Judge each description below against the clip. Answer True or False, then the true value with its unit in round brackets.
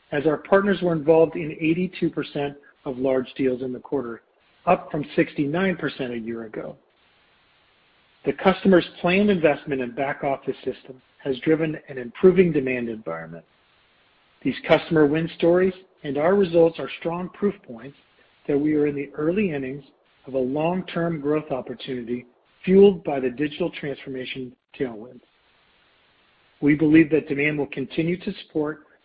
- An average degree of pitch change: True (4.1 semitones)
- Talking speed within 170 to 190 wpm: False (145 wpm)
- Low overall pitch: False (150 Hz)